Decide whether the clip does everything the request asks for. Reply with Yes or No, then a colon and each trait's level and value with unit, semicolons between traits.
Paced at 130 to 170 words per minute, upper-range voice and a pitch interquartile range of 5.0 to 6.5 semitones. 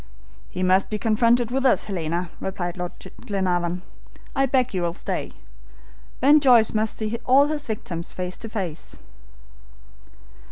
Yes: average, 145 wpm; high, 210 Hz; average, 5.3 semitones